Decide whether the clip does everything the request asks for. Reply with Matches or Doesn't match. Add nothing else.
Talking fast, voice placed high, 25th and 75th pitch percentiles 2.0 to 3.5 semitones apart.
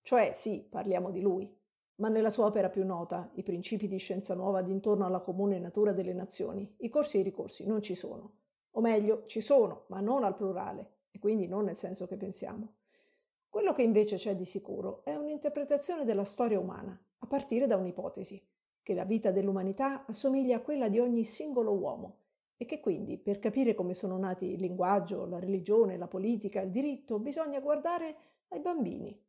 Doesn't match